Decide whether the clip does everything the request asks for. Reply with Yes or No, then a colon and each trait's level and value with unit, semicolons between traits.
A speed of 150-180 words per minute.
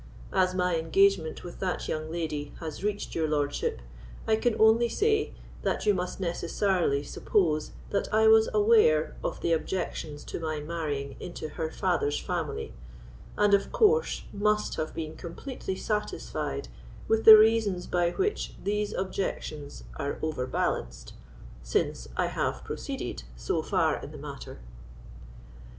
No: average, 140 wpm